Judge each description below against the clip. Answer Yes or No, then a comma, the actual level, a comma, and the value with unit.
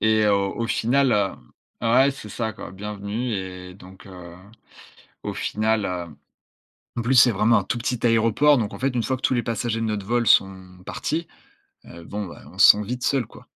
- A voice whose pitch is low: Yes, low, 110 Hz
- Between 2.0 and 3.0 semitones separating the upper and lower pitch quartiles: No, average, 3.6 semitones